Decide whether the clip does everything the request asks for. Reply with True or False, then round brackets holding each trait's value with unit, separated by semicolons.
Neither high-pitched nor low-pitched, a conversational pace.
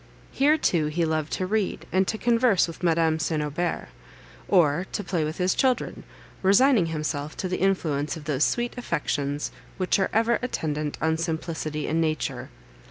True (165 Hz; 165 wpm)